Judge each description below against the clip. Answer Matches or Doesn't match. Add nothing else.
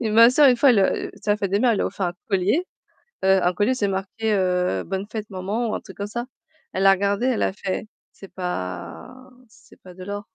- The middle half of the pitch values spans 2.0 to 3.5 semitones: Matches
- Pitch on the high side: Matches